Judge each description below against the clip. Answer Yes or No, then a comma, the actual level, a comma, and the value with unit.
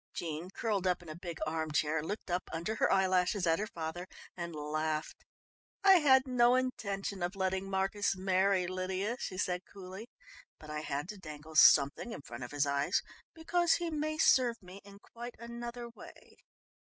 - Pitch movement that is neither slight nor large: No, wide, 6.1 semitones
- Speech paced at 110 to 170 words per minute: No, average, 180 wpm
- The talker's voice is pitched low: No, high, 190 Hz